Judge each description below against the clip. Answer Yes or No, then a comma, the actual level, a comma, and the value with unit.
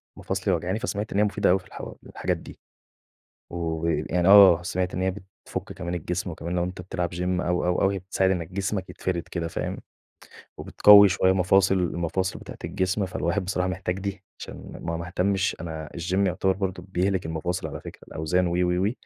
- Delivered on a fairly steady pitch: Yes, narrow, 1.7 semitones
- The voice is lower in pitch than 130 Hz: Yes, very low, 90 Hz